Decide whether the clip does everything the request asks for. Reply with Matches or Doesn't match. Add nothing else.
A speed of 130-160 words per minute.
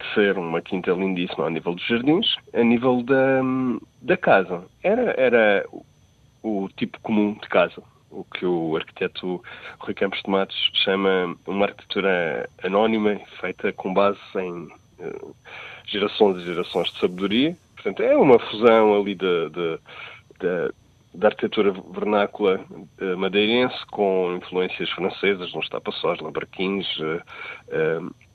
Matches